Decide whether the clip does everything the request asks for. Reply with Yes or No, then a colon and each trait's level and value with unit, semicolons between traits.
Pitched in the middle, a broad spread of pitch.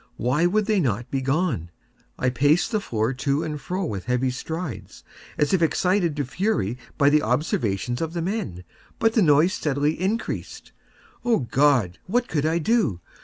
Yes: medium, 150 Hz; wide, 6.3 semitones